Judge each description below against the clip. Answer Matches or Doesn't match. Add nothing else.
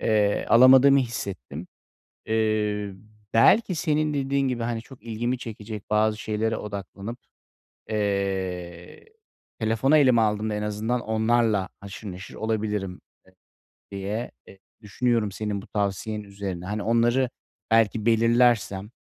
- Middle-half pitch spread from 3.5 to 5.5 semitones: Doesn't match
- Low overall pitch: Matches